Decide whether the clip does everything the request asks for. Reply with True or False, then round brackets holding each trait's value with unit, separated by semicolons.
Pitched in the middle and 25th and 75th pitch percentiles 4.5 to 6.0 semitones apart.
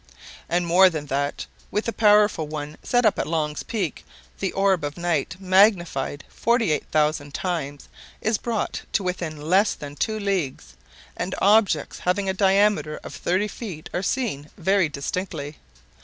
True (180 Hz; 5.0 semitones)